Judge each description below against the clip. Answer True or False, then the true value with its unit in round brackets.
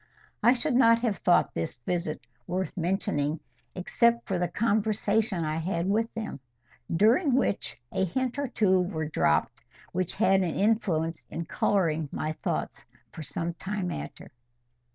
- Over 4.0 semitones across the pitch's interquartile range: True (5.1 semitones)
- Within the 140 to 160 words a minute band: True (150 wpm)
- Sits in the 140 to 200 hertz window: True (190 Hz)